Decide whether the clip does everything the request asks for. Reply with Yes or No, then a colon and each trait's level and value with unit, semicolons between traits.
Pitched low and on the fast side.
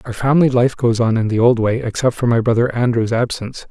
Yes: low, 120 Hz; fast, 245 wpm